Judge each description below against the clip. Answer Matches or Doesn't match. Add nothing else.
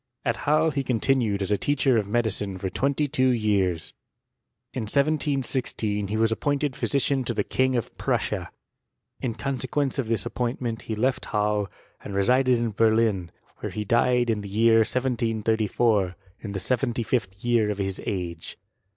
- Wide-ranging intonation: Doesn't match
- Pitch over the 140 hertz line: Doesn't match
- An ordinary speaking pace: Matches